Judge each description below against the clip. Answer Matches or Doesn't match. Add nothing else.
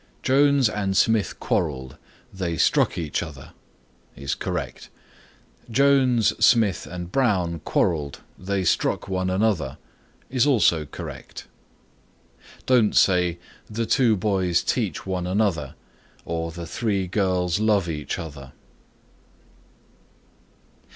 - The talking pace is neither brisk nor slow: Doesn't match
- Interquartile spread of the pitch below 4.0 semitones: Doesn't match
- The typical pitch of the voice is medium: Doesn't match